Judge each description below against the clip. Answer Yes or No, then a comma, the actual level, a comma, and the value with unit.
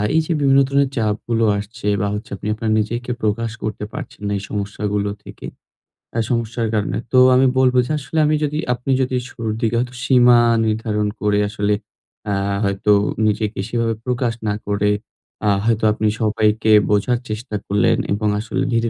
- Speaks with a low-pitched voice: Yes, low, 110 Hz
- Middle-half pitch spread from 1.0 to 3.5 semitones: Yes, average, 2.8 semitones